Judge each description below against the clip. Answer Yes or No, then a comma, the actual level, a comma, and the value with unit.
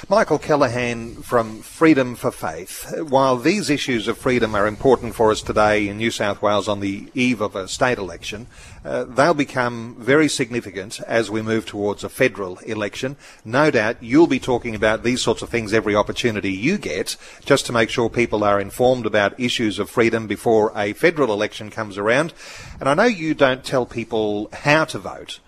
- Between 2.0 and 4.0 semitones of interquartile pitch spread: Yes, average, 3.6 semitones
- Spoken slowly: No, average, 190 wpm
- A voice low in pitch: Yes, low, 115 Hz